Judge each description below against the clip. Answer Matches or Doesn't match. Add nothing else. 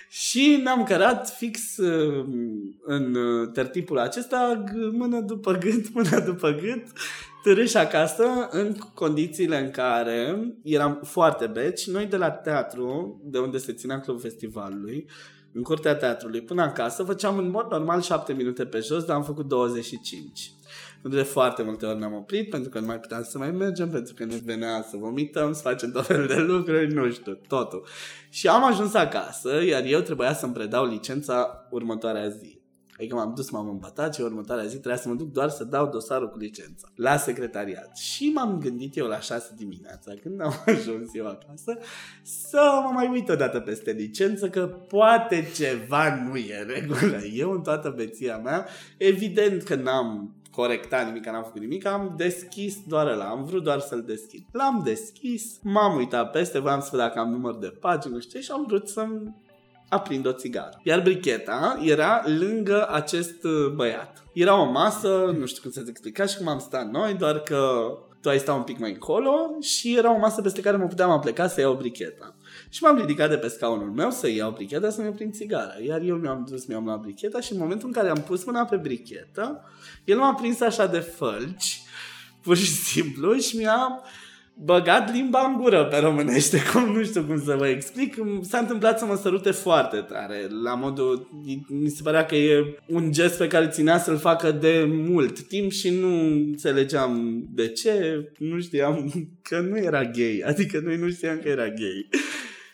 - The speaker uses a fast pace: Matches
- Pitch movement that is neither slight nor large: Doesn't match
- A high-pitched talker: Doesn't match